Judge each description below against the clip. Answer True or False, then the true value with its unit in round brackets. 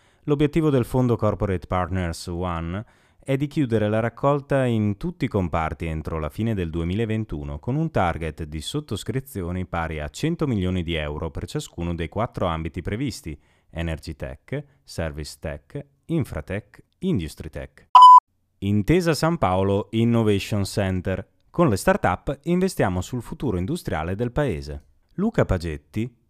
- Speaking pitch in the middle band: False (100 Hz)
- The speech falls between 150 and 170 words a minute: False (135 wpm)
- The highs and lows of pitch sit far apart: True (8.2 semitones)